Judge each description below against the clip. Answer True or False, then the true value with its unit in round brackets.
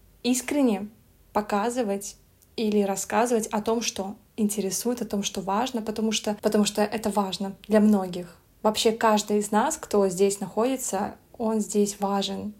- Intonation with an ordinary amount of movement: False (2.0 semitones)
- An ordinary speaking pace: True (145 wpm)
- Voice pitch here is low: False (210 Hz)